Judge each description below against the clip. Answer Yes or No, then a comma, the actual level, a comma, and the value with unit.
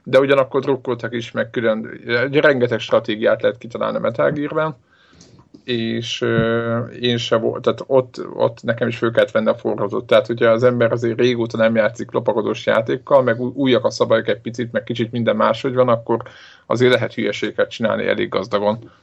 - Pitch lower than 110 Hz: No, low, 120 Hz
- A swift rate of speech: Yes, fast, 175 wpm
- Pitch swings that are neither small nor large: No, narrow, 2.1 semitones